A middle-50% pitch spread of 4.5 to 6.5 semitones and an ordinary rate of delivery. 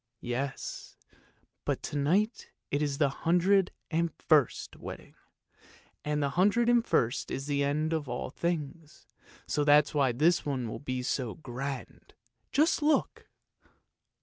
No: average, 3.8 semitones; average, 145 wpm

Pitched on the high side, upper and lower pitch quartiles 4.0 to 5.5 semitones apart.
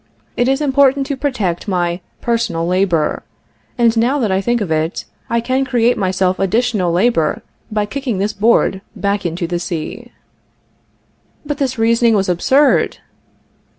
Yes: high, 215 Hz; average, 5.2 semitones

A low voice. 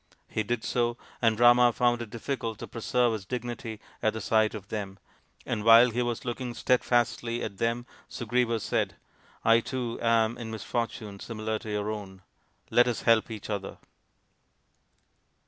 Yes: low, 115 Hz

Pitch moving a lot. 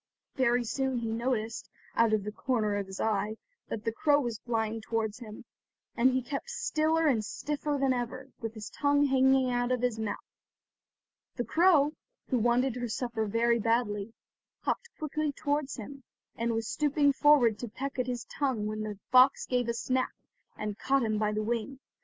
No: average, 3.5 semitones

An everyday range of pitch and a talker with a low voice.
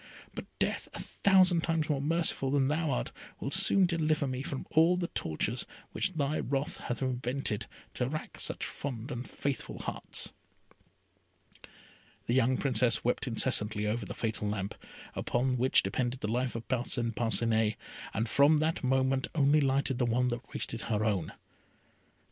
Yes: average, 3.9 semitones; low, 130 Hz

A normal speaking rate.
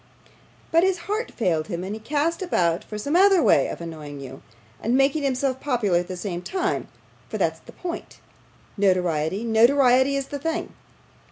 Yes: average, 175 wpm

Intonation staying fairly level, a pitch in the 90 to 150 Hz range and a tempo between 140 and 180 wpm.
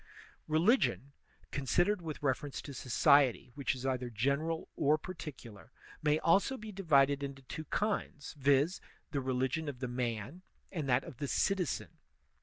No: average, 3.7 semitones; medium, 140 Hz; average, 145 wpm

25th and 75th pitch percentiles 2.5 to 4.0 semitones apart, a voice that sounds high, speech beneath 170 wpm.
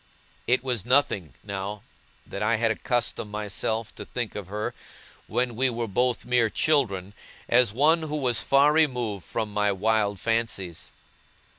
No: average, 3.3 semitones; low, 115 Hz; average, 150 wpm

